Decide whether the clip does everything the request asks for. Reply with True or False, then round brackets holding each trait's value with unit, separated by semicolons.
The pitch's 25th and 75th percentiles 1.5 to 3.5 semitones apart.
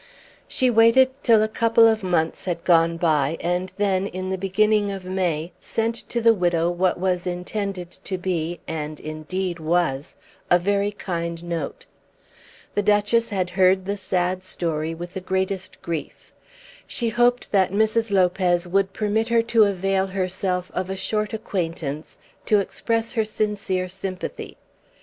True (3.0 semitones)